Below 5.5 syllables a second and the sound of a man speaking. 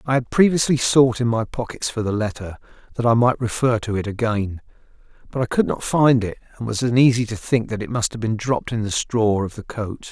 No: 5.6 syllables/s; male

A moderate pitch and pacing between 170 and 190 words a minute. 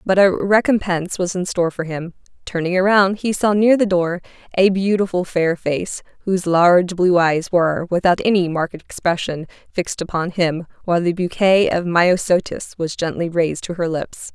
Yes: medium, 180 Hz; average, 175 wpm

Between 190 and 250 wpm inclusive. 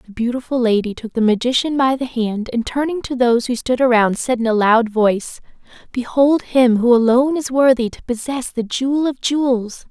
Yes: average, 200 wpm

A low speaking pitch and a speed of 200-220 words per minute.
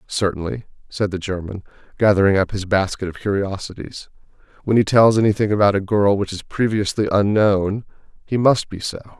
No: low, 100 Hz; average, 165 wpm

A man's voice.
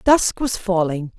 No: female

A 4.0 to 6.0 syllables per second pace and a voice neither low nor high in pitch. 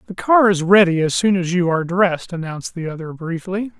Yes: 5.9 syllables/s; medium, 180 Hz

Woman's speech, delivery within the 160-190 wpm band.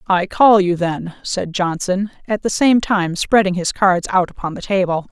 No: female; average, 200 wpm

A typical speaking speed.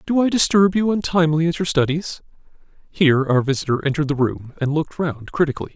Yes: average, 190 wpm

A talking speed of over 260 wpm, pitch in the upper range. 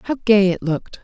No: fast, 230 wpm; high, 205 Hz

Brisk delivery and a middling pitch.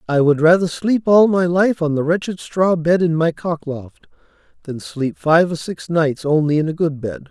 Yes: fast, 220 wpm; medium, 165 Hz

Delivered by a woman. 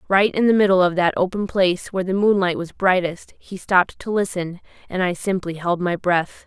Yes: female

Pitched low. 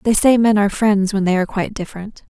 No: high, 205 Hz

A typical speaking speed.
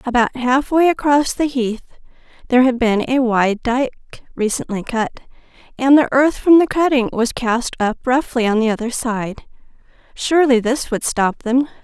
Yes: average, 160 wpm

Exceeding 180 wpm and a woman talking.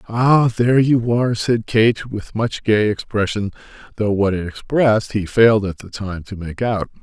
No: average, 190 wpm; male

